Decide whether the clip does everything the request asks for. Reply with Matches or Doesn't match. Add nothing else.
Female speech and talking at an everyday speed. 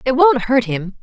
Doesn't match